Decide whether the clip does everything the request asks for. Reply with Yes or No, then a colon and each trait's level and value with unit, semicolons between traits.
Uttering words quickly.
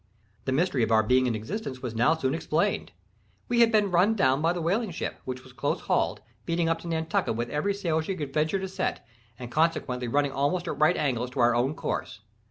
Yes: fast, 225 wpm